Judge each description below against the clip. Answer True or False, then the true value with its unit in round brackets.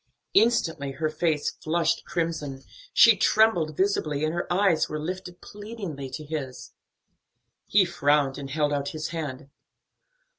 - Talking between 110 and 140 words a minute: True (135 wpm)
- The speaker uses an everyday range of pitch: True (3.6 semitones)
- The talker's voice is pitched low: False (155 Hz)